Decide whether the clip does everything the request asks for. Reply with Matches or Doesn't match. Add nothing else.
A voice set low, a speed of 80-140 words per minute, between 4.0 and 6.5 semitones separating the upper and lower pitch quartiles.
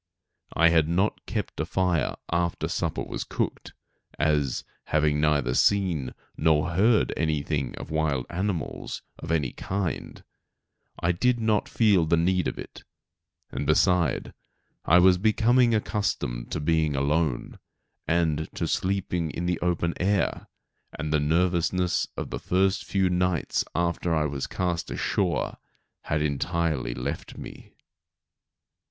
Doesn't match